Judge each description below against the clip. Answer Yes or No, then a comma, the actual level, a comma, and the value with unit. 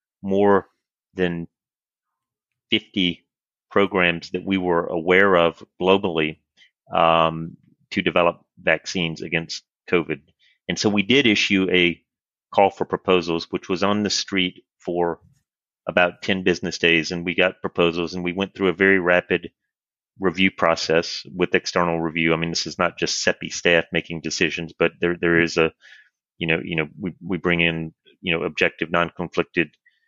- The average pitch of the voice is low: Yes, very low, 90 Hz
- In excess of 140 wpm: Yes, average, 160 wpm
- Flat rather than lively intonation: Yes, narrow, 2.3 semitones